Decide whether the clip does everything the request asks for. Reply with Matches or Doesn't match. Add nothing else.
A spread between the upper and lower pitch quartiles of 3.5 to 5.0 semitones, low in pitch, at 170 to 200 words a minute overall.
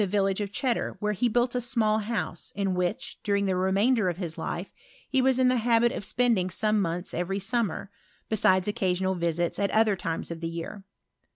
Doesn't match